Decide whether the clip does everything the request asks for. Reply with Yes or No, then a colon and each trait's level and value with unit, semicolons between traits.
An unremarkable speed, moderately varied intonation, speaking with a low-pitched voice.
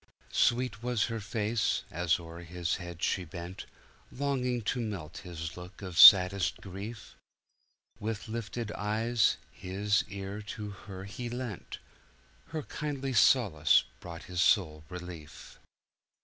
No: slow, 120 wpm; average, 4.5 semitones; low, 100 Hz